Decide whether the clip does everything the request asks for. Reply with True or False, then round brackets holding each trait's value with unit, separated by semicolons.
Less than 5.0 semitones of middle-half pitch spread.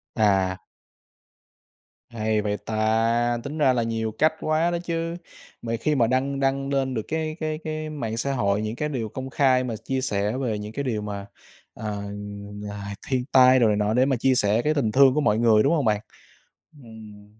True (4.3 semitones)